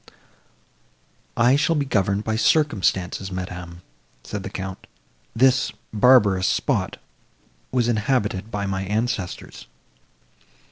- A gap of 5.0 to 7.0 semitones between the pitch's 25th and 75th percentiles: No, average, 4.5 semitones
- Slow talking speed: Yes, slow, 100 wpm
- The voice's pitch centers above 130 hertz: No, low, 105 Hz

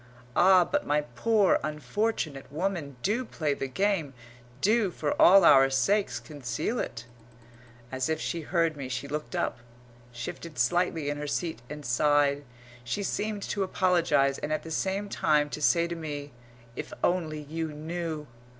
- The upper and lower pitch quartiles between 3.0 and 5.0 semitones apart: Yes, average, 4.2 semitones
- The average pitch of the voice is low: No, medium, 155 Hz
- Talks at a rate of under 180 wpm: Yes, average, 160 wpm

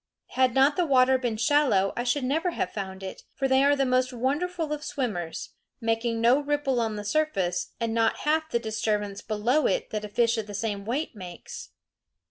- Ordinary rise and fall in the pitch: Yes, average, 5.0 semitones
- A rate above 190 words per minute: Yes, average, 200 wpm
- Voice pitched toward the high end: Yes, high, 240 Hz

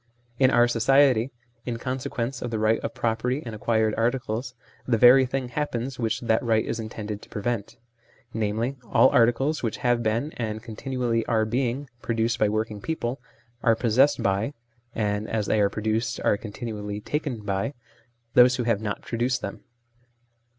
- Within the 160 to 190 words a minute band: Yes, average, 170 wpm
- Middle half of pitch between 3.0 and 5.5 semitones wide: No, narrow, 2.5 semitones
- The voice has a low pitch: Yes, low, 115 Hz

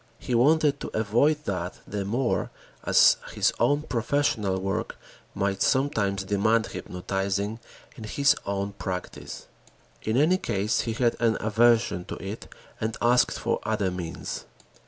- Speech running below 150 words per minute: Yes, slow, 135 wpm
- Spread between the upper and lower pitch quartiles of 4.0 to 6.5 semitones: No, average, 3.5 semitones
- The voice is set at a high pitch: No, low, 110 Hz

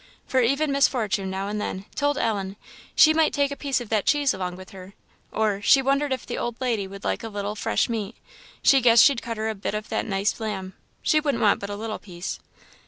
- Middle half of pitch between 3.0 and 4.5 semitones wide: No, average, 5.2 semitones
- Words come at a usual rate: No, fast, 240 wpm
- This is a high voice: Yes, high, 220 Hz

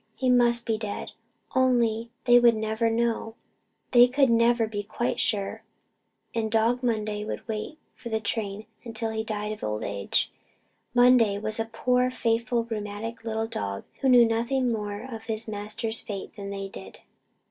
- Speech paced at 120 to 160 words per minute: No, average, 170 wpm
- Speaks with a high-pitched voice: Yes, high, 225 Hz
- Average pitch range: No, narrow, 2.0 semitones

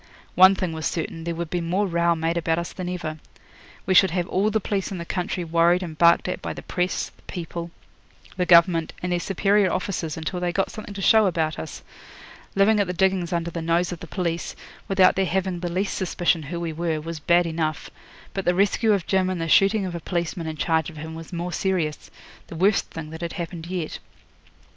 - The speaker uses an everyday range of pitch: No, narrow, 2.2 semitones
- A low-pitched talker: No, medium, 175 Hz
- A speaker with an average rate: No, fast, 225 wpm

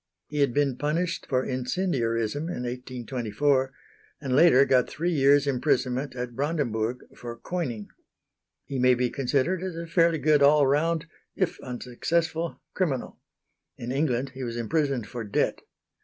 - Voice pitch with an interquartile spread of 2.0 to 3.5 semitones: No, average, 4.0 semitones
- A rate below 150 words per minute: Yes, average, 140 wpm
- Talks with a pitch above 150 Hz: No, low, 135 Hz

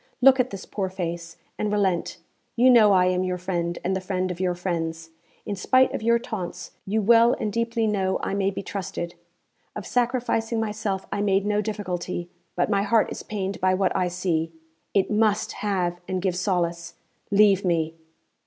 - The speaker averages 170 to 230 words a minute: Yes, average, 185 wpm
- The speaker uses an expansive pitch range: No, average, 2.9 semitones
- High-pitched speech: Yes, high, 195 Hz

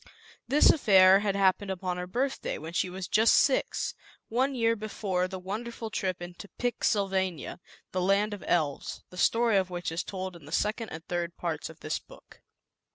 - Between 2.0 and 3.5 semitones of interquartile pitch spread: Yes, average, 3.2 semitones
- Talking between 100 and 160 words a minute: No, average, 185 wpm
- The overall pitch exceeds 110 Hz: Yes, high, 190 Hz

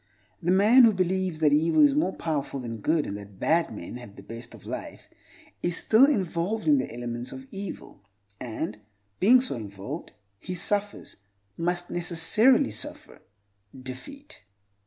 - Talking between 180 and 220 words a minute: No, average, 145 wpm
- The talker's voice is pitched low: No, medium, 165 Hz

